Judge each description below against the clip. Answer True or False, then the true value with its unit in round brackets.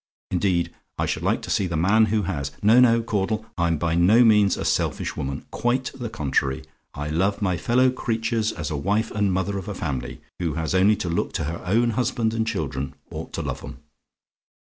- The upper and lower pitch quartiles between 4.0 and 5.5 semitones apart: True (5.0 semitones)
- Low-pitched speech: True (100 Hz)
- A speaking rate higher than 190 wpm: True (205 wpm)